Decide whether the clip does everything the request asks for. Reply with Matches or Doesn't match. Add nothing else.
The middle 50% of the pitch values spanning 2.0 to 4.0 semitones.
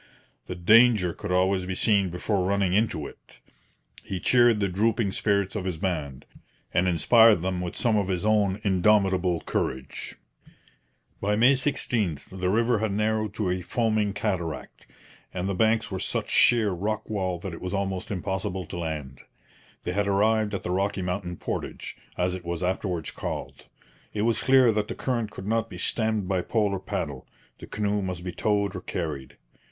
Matches